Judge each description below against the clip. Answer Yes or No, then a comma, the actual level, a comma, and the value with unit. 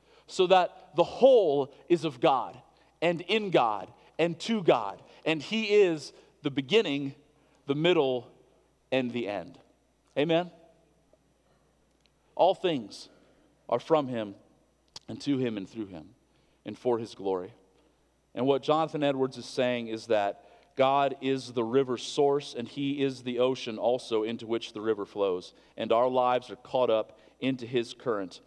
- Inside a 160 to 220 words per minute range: No, average, 150 wpm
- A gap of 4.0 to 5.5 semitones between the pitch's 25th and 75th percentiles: Yes, average, 5.0 semitones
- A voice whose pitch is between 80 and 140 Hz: Yes, low, 135 Hz